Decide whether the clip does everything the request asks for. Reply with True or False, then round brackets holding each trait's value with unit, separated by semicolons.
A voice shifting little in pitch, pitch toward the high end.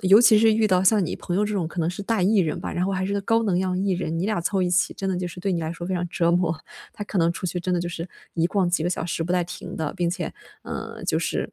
False (2.3 semitones; 180 Hz)